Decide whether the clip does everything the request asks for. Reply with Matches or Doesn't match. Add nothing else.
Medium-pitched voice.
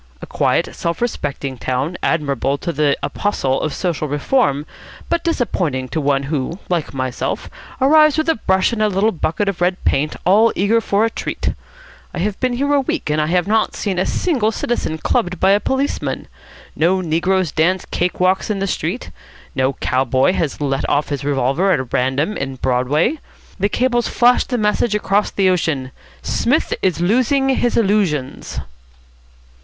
Matches